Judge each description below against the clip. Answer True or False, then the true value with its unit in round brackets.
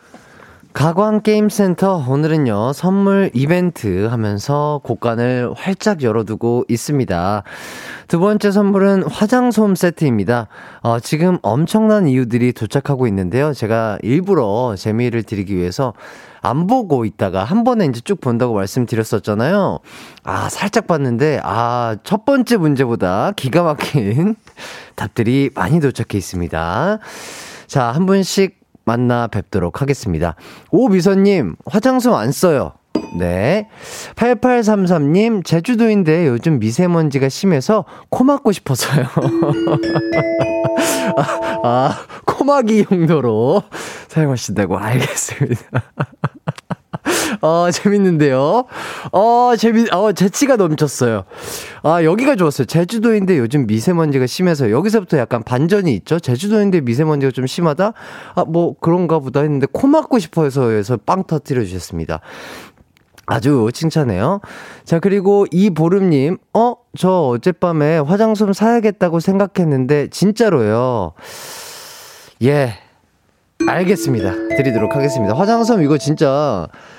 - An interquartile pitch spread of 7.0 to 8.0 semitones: False (8.5 semitones)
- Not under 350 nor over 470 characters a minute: False (275 characters per minute)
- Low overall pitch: False (155 Hz)